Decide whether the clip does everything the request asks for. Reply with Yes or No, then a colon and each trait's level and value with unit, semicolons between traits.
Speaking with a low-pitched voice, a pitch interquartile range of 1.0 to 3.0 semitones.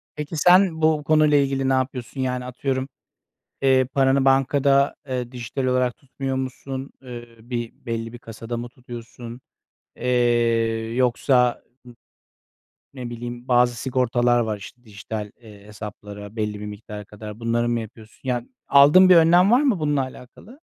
Yes: low, 125 Hz; average, 2.7 semitones